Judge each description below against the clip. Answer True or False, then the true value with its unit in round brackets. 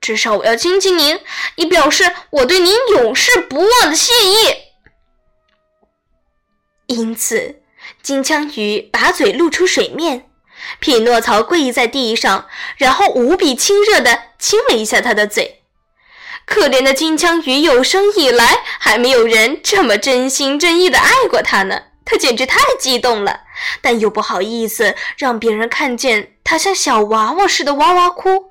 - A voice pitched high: True (310 Hz)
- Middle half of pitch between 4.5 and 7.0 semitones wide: False (8.0 semitones)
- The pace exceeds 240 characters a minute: False (220 characters per minute)